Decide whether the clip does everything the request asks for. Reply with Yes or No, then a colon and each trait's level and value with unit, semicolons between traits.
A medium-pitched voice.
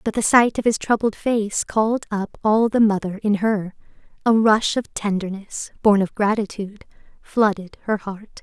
No: high, 210 Hz